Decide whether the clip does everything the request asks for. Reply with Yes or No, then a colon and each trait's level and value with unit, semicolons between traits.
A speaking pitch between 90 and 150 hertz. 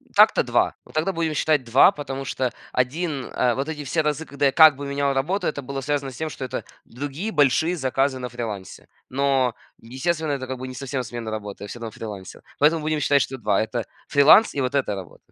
Yes: low, 135 Hz